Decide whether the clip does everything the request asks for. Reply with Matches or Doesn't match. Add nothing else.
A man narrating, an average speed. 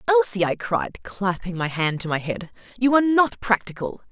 Doesn't match